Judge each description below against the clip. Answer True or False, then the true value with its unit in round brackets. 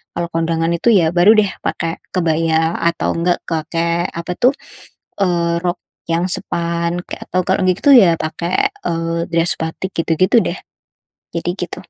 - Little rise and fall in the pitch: True (1.5 semitones)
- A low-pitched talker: False (170 Hz)